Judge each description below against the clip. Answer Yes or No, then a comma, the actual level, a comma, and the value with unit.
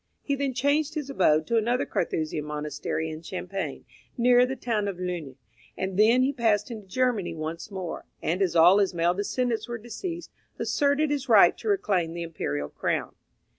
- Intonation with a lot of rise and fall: Yes, wide, 7.0 semitones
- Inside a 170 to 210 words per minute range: Yes, average, 175 wpm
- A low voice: No, high, 205 Hz